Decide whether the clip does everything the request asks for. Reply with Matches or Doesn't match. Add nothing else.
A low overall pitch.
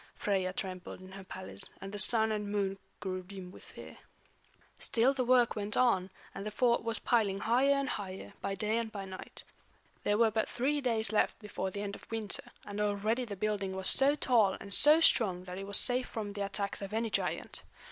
Doesn't match